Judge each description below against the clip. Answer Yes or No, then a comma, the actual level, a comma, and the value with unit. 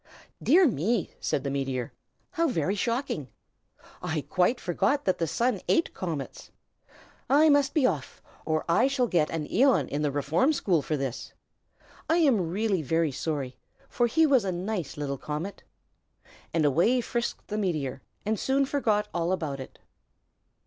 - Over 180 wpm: No, average, 160 wpm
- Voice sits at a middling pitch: Yes, medium, 180 Hz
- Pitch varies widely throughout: Yes, wide, 8.7 semitones